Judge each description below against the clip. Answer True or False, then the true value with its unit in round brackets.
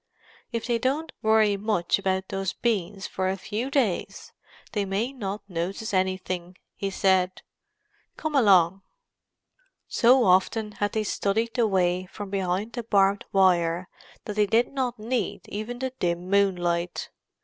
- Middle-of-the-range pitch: False (200 Hz)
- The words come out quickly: False (145 wpm)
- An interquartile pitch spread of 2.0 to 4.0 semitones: True (3.3 semitones)